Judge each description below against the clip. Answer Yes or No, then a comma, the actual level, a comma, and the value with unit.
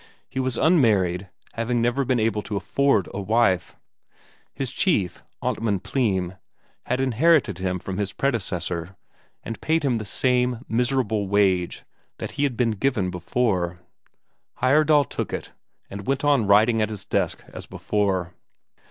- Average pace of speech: Yes, average, 145 wpm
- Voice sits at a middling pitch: No, low, 110 Hz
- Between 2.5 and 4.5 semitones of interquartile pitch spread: No, average, 5.2 semitones